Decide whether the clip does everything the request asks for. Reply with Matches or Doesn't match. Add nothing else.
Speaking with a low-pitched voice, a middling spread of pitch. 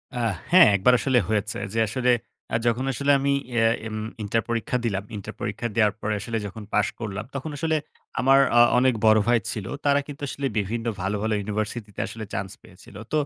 Matches